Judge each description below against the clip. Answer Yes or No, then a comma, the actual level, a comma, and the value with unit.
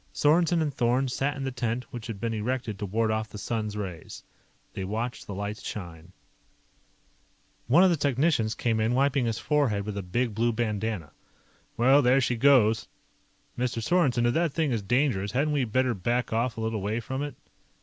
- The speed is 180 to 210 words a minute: Yes, average, 190 wpm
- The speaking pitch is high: No, low, 120 Hz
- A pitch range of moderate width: Yes, average, 3.8 semitones